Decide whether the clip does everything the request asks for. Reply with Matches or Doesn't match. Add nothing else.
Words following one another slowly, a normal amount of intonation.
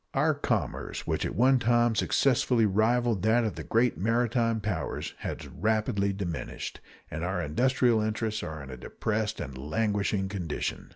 Doesn't match